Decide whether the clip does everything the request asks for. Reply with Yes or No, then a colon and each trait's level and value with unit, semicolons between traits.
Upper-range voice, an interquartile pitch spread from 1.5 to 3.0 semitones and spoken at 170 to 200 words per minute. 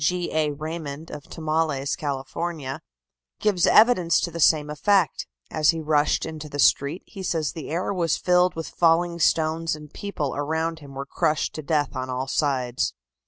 No: medium, 155 Hz; narrow, 2.6 semitones; average, 175 wpm